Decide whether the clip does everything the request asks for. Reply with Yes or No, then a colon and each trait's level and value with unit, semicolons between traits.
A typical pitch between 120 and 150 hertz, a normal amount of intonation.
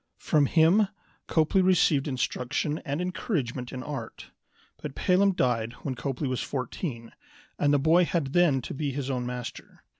Yes: medium, 140 Hz; average, 4.5 semitones